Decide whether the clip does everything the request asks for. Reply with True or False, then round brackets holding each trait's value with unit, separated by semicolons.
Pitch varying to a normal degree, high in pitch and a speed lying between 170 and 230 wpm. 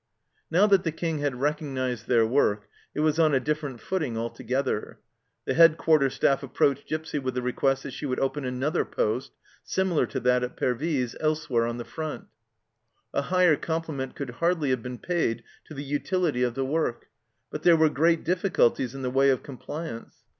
False (4.1 semitones; 140 Hz; 190 wpm)